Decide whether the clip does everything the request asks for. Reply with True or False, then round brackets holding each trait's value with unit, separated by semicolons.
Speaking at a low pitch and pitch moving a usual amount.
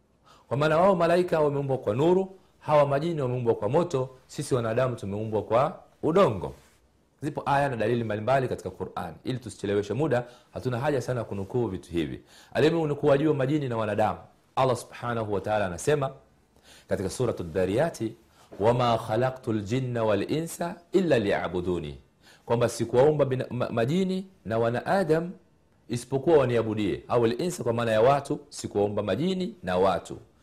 False (120 Hz; 5.8 semitones)